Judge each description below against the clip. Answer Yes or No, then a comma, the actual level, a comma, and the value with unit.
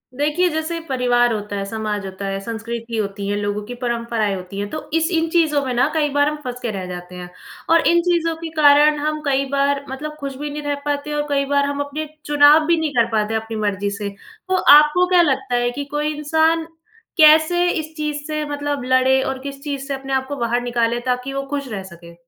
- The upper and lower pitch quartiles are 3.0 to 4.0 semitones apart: No, average, 4.7 semitones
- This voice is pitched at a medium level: No, very high, 275 Hz